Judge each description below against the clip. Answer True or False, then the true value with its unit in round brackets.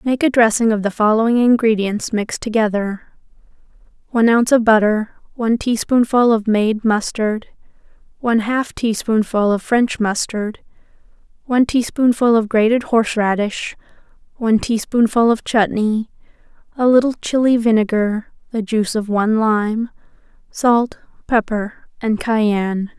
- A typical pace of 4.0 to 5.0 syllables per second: True (4.8 syllables/s)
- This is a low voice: False (225 Hz)